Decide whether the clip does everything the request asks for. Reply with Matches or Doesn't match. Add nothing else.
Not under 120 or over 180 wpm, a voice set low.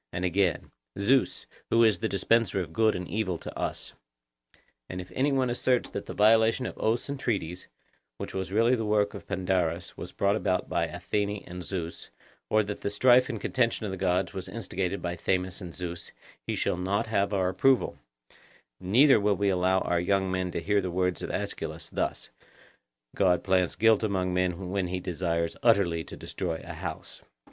Doesn't match